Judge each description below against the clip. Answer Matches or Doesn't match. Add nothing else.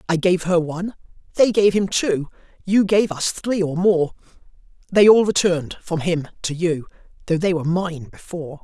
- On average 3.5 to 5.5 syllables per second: Matches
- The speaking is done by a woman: Doesn't match